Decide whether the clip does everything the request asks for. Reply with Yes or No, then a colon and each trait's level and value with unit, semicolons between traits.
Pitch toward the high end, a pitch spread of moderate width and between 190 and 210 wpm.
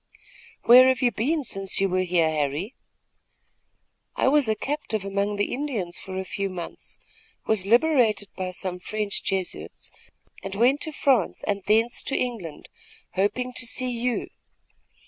No: high, 210 Hz; average, 4.9 semitones; average, 150 wpm